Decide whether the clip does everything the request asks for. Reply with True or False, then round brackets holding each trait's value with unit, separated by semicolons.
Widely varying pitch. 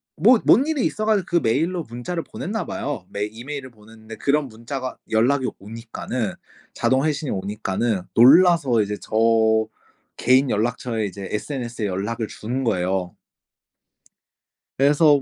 False (5.0 semitones)